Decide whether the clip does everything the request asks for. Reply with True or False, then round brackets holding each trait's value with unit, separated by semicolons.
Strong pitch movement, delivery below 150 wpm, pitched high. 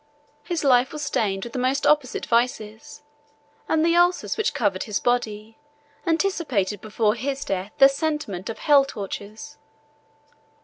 True (5.8 semitones; 140 wpm; 245 Hz)